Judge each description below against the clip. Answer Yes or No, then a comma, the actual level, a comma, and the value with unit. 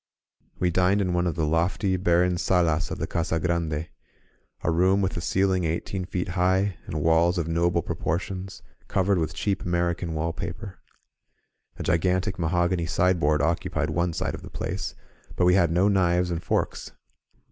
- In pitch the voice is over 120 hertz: No, very low, 90 Hz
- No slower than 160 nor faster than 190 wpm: Yes, average, 165 wpm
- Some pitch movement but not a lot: No, narrow, 1.8 semitones